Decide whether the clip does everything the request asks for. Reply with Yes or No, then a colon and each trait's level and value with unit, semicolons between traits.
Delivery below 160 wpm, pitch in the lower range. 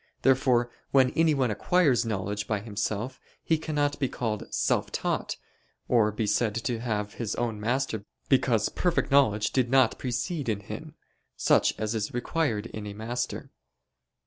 Yes: average, 150 wpm; low, 120 Hz